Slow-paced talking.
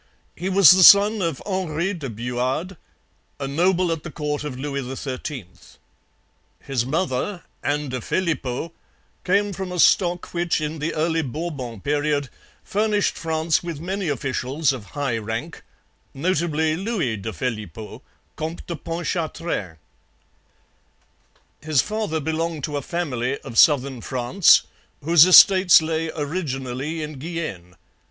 Yes: slow, 130 wpm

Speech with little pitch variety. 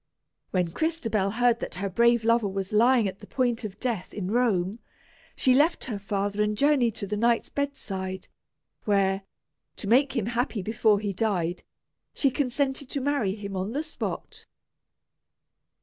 No: average, 4.1 semitones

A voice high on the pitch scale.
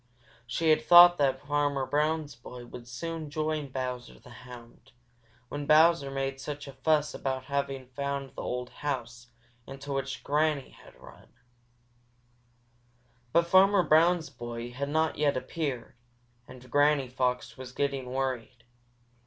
No: medium, 140 Hz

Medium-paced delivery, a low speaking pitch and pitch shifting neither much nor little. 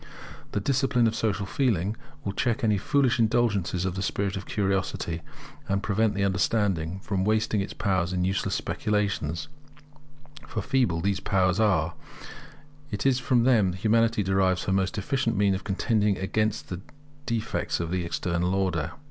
Yes: average, 165 wpm; low, 100 Hz; average, 3.0 semitones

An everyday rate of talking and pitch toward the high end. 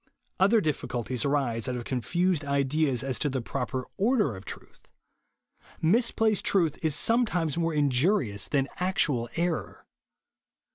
No: average, 150 wpm; medium, 145 Hz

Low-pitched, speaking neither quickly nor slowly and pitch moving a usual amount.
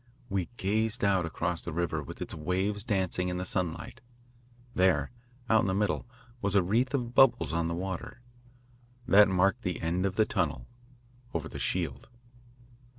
Yes: very low, 95 Hz; average, 165 wpm; average, 3.2 semitones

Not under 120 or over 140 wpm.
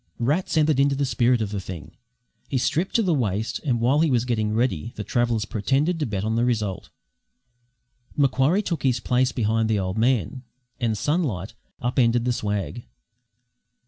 No: average, 175 wpm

